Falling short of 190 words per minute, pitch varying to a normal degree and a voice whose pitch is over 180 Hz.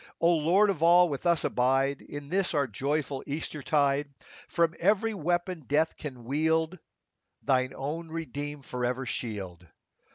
No: average, 140 wpm; average, 3.8 semitones; medium, 150 Hz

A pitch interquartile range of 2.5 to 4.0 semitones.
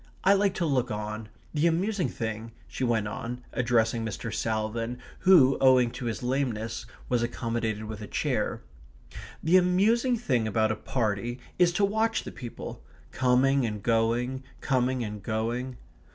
Yes: average, 3.6 semitones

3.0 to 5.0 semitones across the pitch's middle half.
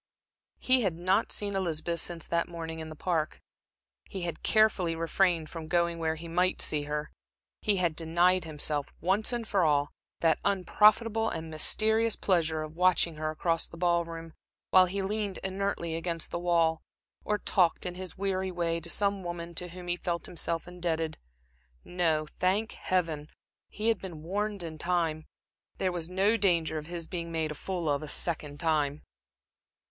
No: narrow, 2.6 semitones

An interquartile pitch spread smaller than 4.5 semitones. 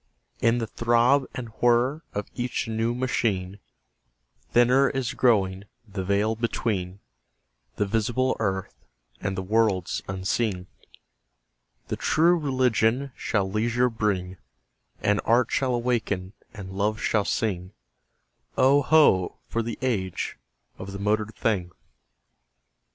Yes: average, 3.8 semitones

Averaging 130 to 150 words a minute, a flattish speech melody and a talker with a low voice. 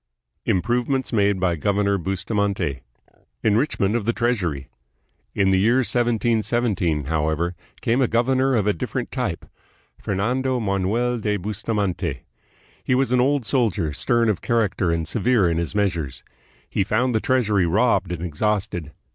No: average, 145 wpm; average, 4.8 semitones; low, 105 Hz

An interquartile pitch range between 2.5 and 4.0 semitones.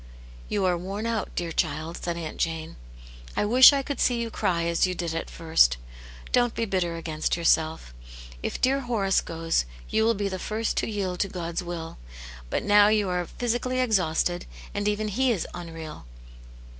No: average, 4.7 semitones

